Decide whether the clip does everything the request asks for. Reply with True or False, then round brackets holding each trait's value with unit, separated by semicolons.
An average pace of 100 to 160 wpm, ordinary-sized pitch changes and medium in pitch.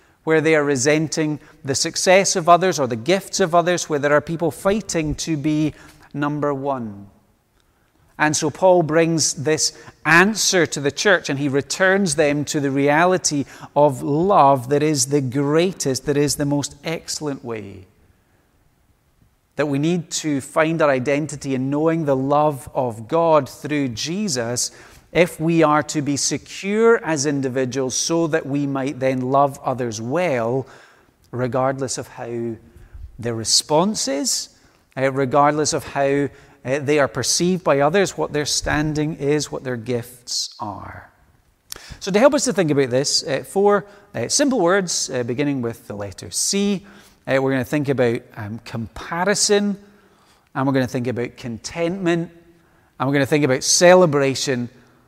True (150 wpm; 3.9 semitones; 145 Hz)